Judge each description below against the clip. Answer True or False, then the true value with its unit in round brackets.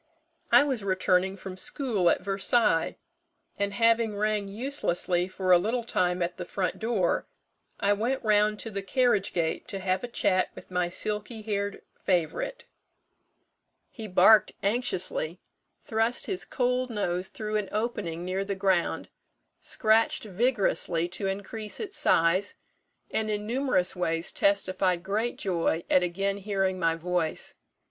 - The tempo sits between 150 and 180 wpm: False (140 wpm)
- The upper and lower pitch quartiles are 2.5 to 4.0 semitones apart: True (3.3 semitones)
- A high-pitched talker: True (200 Hz)